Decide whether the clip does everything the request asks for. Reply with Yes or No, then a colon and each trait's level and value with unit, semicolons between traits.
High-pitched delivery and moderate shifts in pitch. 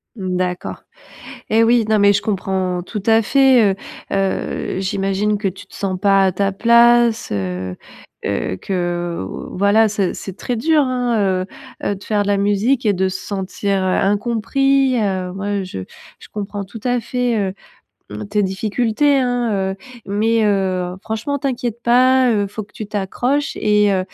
Yes: high, 205 Hz; average, 3.5 semitones